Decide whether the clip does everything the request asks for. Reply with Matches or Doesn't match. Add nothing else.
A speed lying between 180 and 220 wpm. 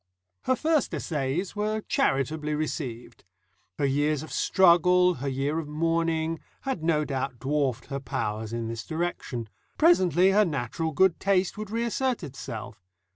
Doesn't match